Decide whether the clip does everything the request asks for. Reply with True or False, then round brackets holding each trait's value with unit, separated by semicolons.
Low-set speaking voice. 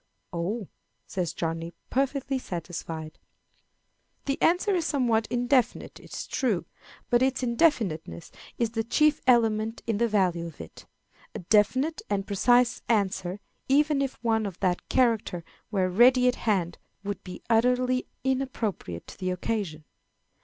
False (225 Hz)